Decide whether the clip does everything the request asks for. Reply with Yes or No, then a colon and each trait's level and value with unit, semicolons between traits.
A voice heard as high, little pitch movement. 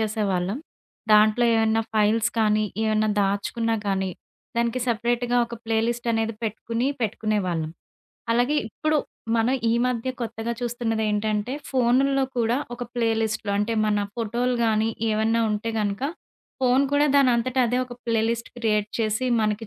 Yes: high, 225 Hz; narrow, 2.0 semitones